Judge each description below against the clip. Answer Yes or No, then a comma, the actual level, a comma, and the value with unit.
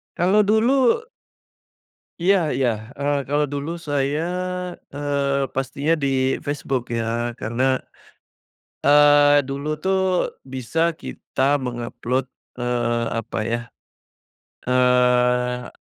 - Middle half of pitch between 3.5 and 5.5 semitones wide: No, average, 2.9 semitones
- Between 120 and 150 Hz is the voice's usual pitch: Yes, medium, 140 Hz